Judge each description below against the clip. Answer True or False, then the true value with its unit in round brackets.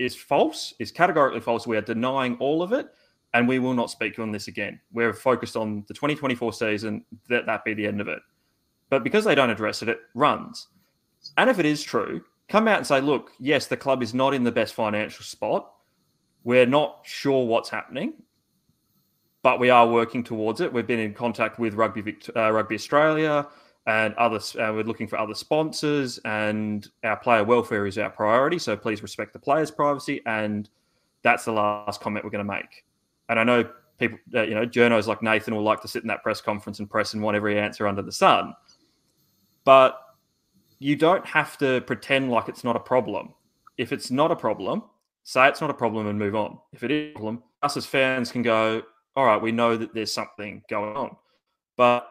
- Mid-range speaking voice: False (115 Hz)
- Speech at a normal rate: False (210 wpm)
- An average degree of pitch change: True (3.4 semitones)